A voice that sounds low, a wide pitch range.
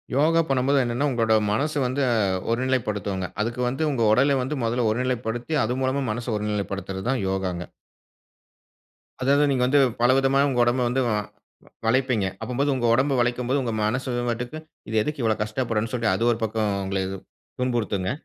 No: low, 120 Hz; average, 3.4 semitones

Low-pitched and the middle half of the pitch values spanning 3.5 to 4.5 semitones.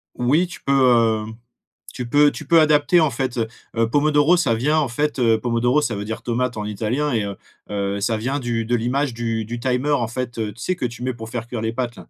Yes: low, 120 Hz; average, 3.8 semitones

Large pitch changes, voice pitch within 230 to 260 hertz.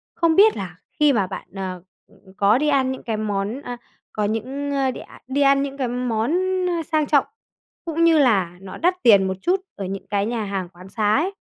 Yes: wide, 6.3 semitones; high, 240 Hz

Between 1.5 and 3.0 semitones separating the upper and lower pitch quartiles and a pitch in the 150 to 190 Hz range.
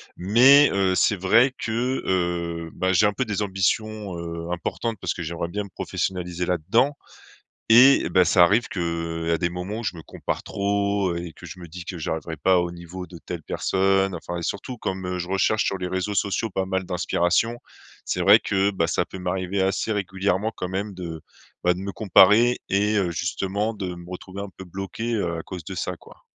No: average, 2.7 semitones; very low, 95 Hz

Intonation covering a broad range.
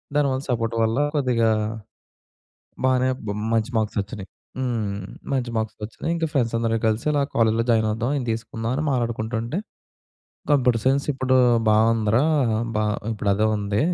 No: average, 2.9 semitones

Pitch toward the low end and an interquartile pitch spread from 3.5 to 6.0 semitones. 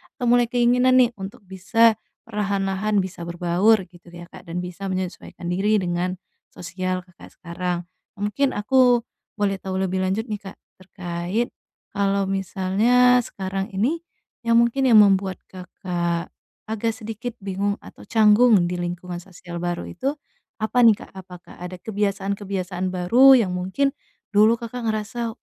No: high, 195 Hz; average, 3.9 semitones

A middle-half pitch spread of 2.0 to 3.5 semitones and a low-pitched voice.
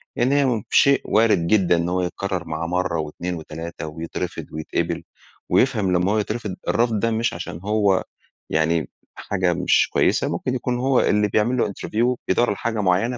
No: average, 5.1 semitones; low, 100 Hz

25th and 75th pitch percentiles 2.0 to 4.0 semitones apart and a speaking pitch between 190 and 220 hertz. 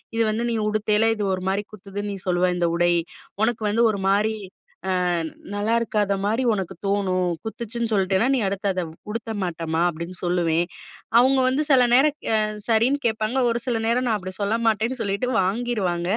Yes: average, 3.6 semitones; high, 210 Hz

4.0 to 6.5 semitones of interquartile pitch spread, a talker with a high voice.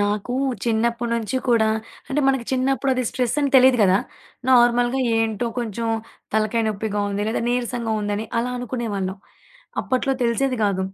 No: average, 2.8 semitones; high, 235 Hz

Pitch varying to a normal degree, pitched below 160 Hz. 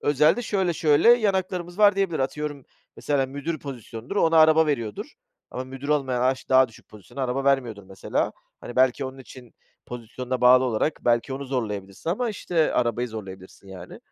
Yes: average, 4.6 semitones; low, 135 Hz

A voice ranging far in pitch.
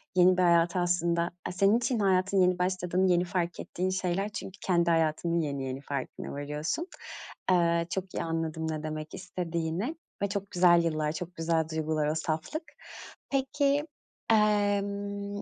No: average, 3.4 semitones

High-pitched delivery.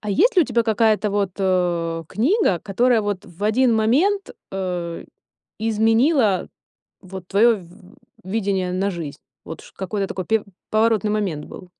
Yes: high, 205 Hz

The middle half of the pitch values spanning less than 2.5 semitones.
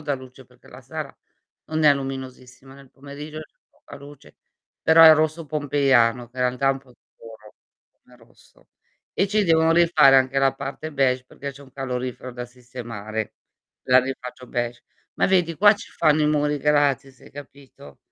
No: average, 2.8 semitones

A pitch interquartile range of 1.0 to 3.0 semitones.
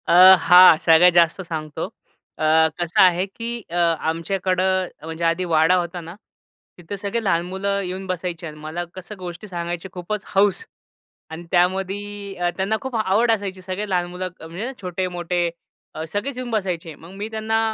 Yes: average, 2.7 semitones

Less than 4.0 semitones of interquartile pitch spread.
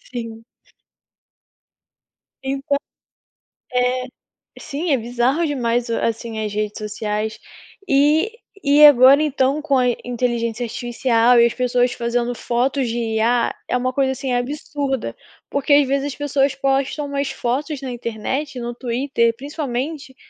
Yes: average, 3.0 semitones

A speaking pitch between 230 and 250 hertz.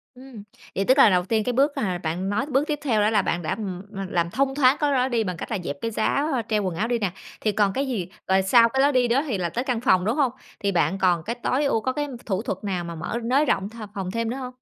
No: high, 220 Hz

